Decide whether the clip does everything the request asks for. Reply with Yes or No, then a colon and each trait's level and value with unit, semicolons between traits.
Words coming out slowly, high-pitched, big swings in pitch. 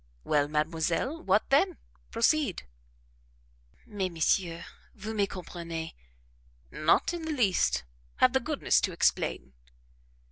Yes: slow, 110 wpm; high, 195 Hz; wide, 8.1 semitones